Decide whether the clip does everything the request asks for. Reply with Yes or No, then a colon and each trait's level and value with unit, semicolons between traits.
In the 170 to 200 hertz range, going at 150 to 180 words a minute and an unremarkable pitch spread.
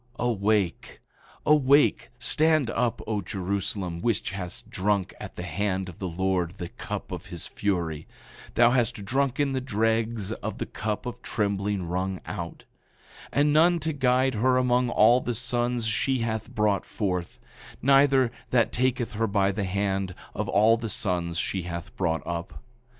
No: low, 110 Hz; average, 160 wpm; average, 4.6 semitones